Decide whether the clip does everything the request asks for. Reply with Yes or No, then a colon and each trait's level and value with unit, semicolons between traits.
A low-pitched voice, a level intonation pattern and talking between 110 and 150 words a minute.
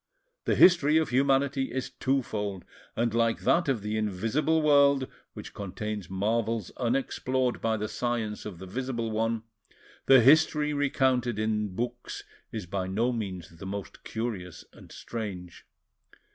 No: low, 115 Hz; average, 4.1 semitones; average, 140 wpm